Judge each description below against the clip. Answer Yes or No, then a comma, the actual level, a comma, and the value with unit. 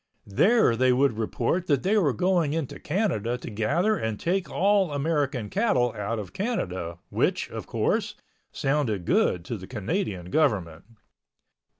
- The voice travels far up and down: Yes, wide, 8.9 semitones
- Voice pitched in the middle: No, low, 130 Hz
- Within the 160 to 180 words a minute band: No, average, 150 wpm